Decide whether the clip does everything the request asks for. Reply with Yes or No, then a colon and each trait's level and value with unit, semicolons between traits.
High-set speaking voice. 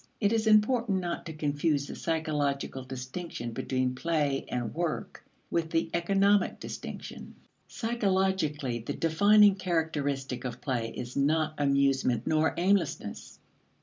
No: medium, 155 Hz